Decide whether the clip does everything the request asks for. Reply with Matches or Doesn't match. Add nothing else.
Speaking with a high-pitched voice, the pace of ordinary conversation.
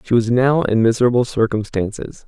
Doesn't match